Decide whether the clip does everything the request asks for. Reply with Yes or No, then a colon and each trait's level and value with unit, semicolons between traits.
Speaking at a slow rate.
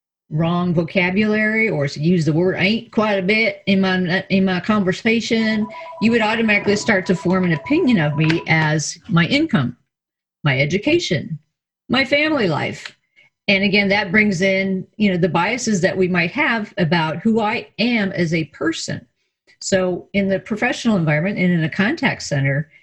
No: average, 170 wpm